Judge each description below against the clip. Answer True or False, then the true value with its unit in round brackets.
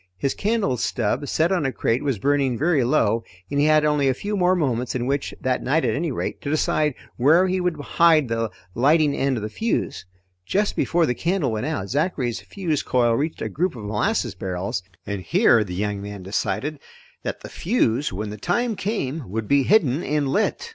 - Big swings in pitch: True (6.2 semitones)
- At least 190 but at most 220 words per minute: True (205 wpm)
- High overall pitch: False (140 Hz)